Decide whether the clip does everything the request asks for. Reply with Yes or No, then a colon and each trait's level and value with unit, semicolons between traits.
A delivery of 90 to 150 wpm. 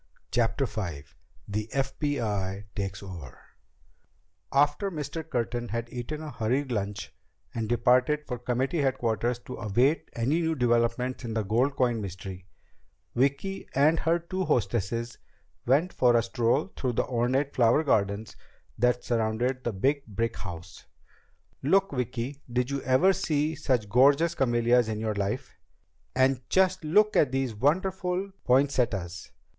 Yes: average, 140 wpm